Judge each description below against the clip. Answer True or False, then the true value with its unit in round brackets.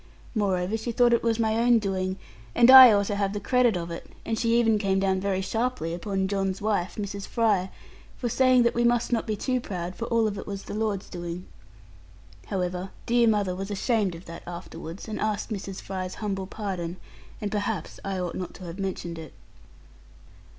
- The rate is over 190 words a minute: True (200 wpm)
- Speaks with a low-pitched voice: False (200 Hz)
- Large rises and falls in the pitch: False (3.3 semitones)